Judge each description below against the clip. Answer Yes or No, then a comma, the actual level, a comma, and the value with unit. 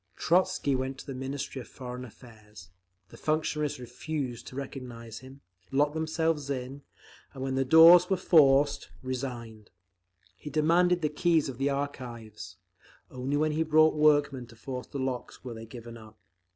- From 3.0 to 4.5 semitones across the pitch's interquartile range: Yes, average, 3.6 semitones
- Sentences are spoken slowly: No, average, 160 wpm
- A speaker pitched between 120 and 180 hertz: Yes, low, 135 Hz